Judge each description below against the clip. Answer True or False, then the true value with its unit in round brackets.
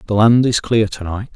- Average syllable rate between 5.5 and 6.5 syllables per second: False (5.2 syllables/s)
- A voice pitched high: False (110 Hz)